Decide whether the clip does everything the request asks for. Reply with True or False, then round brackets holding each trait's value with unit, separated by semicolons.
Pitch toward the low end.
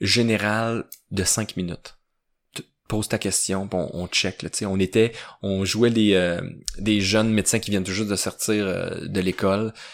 True (100 Hz)